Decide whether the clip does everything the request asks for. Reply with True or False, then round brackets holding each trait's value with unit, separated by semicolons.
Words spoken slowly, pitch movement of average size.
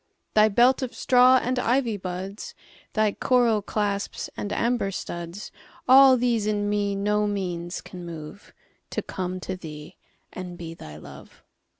True (130 wpm; 4.6 semitones)